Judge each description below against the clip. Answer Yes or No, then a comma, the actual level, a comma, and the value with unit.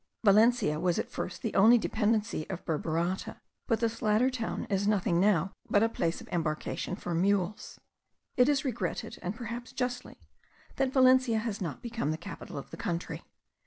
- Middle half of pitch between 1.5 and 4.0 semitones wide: No, average, 5.1 semitones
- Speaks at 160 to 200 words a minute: Yes, average, 170 wpm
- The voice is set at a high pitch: Yes, high, 210 Hz